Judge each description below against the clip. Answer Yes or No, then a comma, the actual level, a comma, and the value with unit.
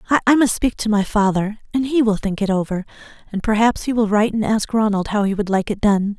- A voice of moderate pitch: No, high, 215 Hz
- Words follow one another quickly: Yes, fast, 250 wpm